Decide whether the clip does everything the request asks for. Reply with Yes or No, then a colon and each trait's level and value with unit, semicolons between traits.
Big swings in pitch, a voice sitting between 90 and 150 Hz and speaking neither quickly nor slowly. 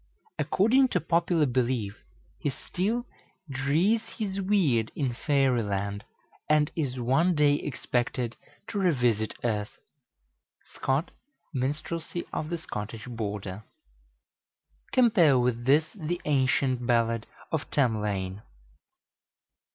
No: wide, 6.2 semitones; low, 135 Hz; slow, 105 wpm